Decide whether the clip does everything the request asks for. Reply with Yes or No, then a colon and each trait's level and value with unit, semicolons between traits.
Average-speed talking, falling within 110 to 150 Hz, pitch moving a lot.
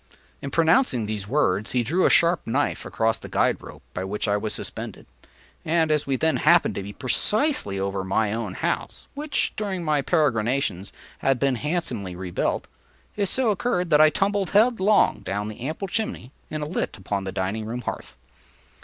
Yes: average, 180 wpm; low, 135 Hz; wide, 9.0 semitones